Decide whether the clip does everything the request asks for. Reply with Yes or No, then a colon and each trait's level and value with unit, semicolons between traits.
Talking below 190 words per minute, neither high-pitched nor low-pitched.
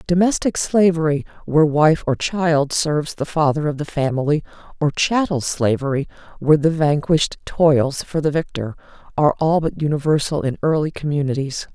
Yes: average, 150 wpm; medium, 150 Hz